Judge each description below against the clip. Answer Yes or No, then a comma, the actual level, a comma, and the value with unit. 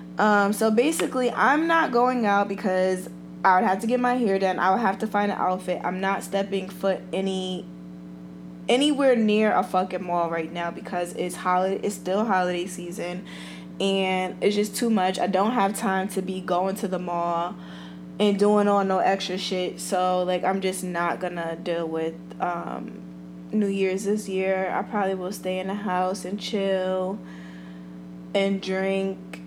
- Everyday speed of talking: Yes, average, 175 wpm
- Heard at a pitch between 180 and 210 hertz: Yes, medium, 185 Hz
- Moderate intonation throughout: No, narrow, 2.3 semitones